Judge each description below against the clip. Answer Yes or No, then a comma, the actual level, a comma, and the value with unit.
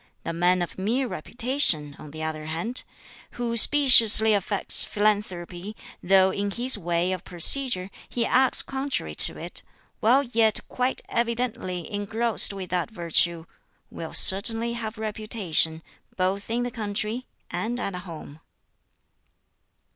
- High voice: Yes, high, 205 Hz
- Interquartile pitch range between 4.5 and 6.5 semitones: Yes, average, 4.8 semitones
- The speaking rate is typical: No, slow, 130 wpm